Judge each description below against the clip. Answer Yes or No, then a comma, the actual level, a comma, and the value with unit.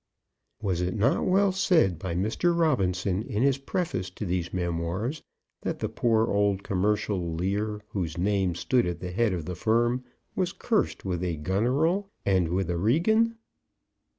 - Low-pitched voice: Yes, low, 100 Hz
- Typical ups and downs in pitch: No, wide, 6.3 semitones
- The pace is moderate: Yes, average, 160 wpm